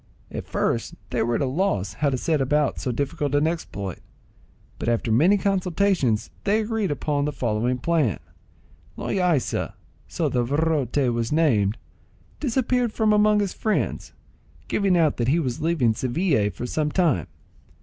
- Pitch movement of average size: No, wide, 7.1 semitones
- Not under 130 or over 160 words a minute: Yes, average, 150 wpm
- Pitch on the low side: No, medium, 150 Hz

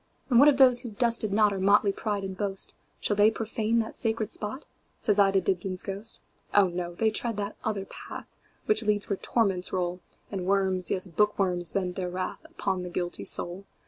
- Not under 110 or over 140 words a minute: No, average, 175 wpm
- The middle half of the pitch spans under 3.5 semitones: Yes, average, 2.7 semitones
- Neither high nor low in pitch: No, high, 200 Hz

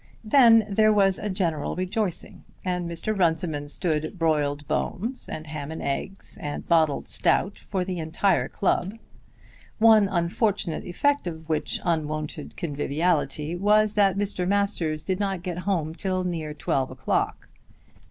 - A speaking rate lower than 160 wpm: Yes, average, 140 wpm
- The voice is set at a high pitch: No, medium, 175 Hz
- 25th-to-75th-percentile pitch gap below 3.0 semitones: No, average, 4.2 semitones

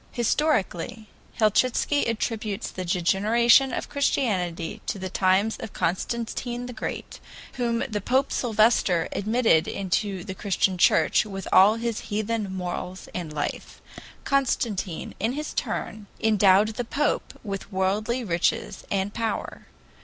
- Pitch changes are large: No, average, 3.9 semitones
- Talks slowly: Yes, slow, 125 wpm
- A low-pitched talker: No, high, 210 Hz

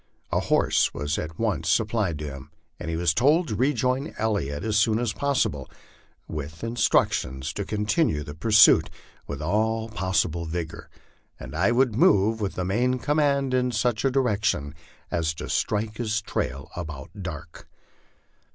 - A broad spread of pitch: Yes, wide, 6.7 semitones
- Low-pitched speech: Yes, low, 105 Hz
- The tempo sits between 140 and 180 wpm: Yes, average, 150 wpm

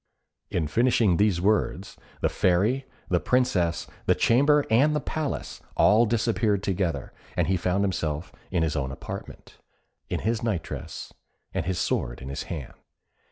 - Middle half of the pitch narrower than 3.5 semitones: No, wide, 5.6 semitones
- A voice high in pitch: No, very low, 95 Hz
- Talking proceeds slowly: No, average, 155 wpm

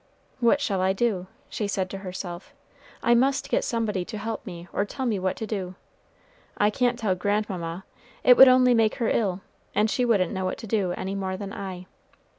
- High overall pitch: Yes, high, 205 Hz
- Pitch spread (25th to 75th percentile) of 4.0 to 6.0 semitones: No, average, 3.6 semitones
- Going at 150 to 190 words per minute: No, fast, 205 wpm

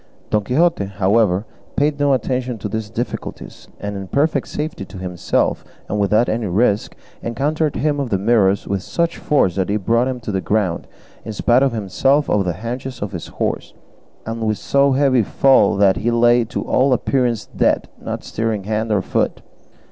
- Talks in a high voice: No, low, 115 Hz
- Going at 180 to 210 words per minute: Yes, average, 185 wpm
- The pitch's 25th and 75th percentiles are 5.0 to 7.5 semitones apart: No, average, 4.6 semitones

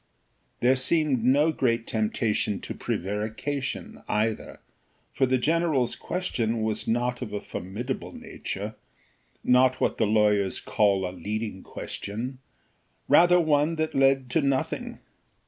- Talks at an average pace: No, slow, 125 wpm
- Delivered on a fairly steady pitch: No, average, 4.5 semitones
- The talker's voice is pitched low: Yes, low, 125 Hz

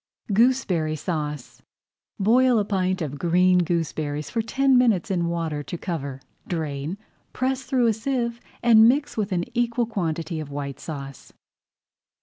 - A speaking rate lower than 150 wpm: Yes, average, 140 wpm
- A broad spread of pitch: Yes, wide, 7.1 semitones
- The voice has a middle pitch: Yes, medium, 180 Hz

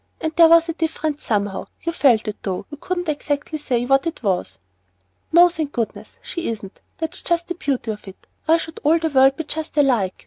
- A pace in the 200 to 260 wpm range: Yes, fast, 205 wpm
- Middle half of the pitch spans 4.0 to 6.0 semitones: Yes, wide, 5.6 semitones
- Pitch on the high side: Yes, very high, 295 Hz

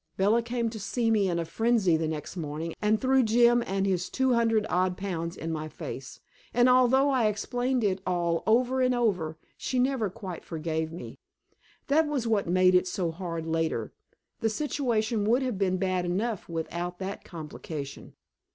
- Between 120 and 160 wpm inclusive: No, average, 180 wpm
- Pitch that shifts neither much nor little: No, wide, 5.8 semitones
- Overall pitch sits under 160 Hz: No, high, 195 Hz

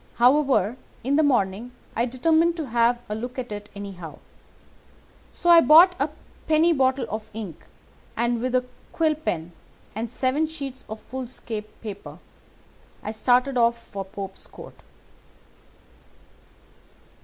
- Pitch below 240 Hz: No, high, 245 Hz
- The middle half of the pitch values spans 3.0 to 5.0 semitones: Yes, average, 4.6 semitones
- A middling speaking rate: No, slow, 130 wpm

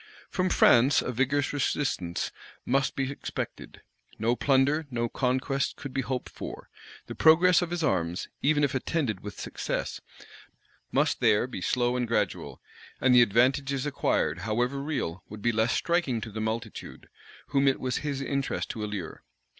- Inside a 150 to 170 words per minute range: Yes, average, 160 wpm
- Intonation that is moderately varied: Yes, average, 3.8 semitones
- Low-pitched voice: Yes, low, 130 Hz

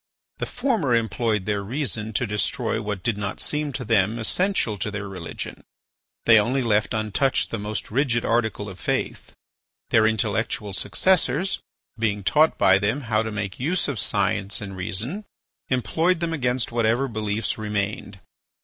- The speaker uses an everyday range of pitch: Yes, average, 3.8 semitones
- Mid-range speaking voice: No, low, 110 Hz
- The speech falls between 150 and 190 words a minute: Yes, average, 155 wpm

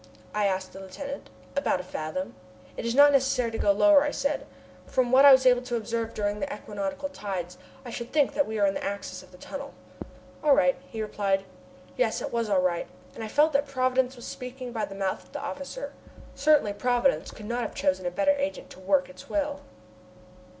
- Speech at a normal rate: No, fast, 220 wpm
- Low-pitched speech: No, high, 235 Hz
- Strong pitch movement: Yes, wide, 6.1 semitones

